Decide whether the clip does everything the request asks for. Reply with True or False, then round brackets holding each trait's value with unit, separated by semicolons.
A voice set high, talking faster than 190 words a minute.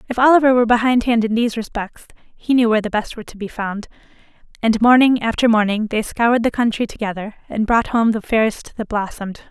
True (225 Hz; 200 wpm)